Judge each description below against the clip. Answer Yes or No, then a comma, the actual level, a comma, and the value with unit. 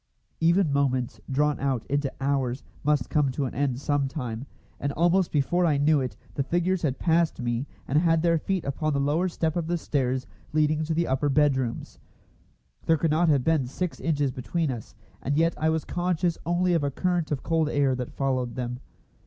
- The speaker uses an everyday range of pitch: Yes, average, 3.6 semitones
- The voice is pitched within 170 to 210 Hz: No, medium, 145 Hz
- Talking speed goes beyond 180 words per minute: Yes, average, 200 wpm